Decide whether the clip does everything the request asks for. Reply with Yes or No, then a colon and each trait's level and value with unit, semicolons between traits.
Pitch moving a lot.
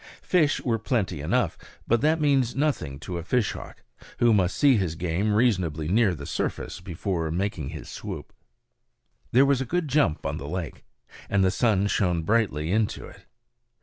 Yes: wide, 6.5 semitones